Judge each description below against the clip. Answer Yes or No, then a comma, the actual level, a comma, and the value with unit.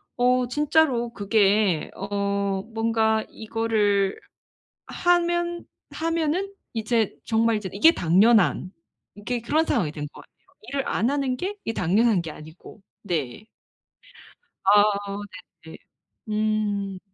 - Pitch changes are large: No, average, 4.1 semitones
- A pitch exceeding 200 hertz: Yes, high, 220 Hz